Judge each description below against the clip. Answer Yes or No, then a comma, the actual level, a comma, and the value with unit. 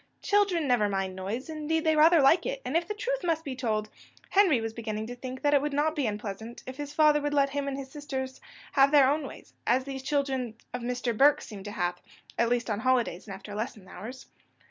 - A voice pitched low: No, very high, 265 Hz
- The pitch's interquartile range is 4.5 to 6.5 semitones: Yes, average, 4.9 semitones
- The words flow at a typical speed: No, fast, 235 wpm